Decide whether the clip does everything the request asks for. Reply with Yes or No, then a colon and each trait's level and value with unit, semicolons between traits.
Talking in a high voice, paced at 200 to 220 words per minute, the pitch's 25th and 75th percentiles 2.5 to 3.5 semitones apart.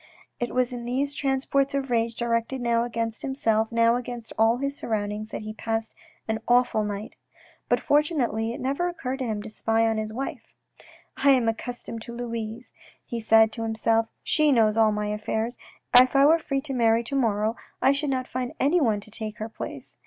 Yes: high, 230 Hz; fast, 205 wpm; average, 2.9 semitones